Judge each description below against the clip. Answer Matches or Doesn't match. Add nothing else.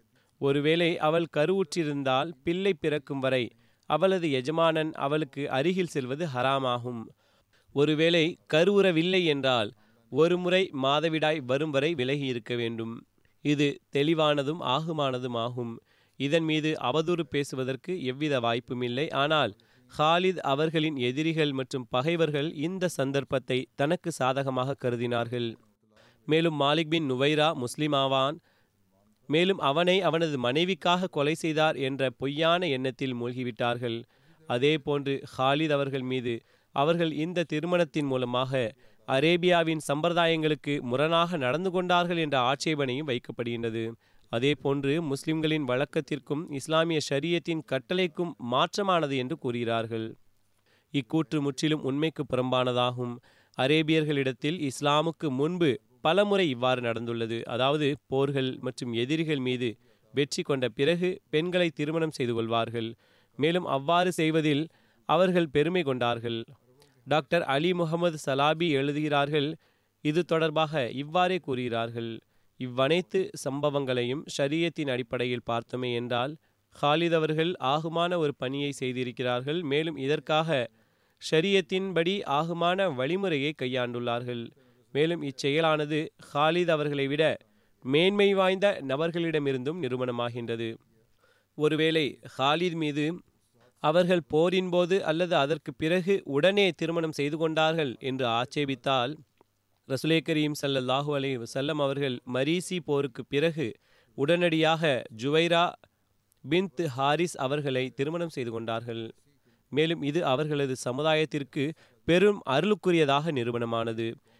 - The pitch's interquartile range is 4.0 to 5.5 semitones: Matches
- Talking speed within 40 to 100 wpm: Matches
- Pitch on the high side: Doesn't match